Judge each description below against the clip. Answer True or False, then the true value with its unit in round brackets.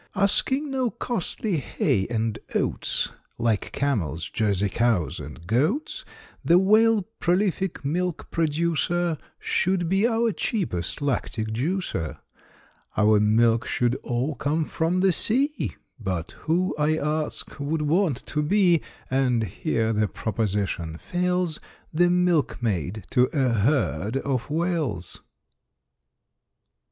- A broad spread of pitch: True (8.2 semitones)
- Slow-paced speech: True (115 wpm)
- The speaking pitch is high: False (150 Hz)